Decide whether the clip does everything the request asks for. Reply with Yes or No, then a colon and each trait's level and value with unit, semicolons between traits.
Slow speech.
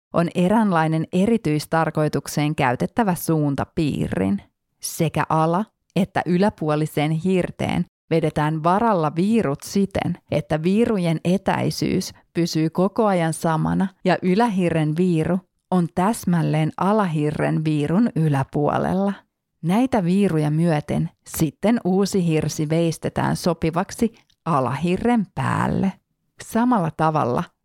Yes: slow, 90 wpm